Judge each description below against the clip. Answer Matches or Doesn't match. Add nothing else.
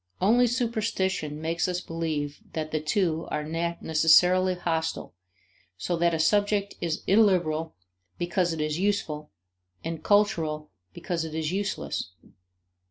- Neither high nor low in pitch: Matches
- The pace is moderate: Doesn't match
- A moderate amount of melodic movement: Matches